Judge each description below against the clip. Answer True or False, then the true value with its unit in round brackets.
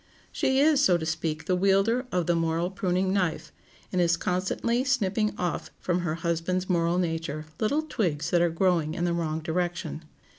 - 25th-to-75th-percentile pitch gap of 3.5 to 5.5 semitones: False (2.7 semitones)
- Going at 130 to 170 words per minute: False (180 wpm)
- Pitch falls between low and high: True (175 Hz)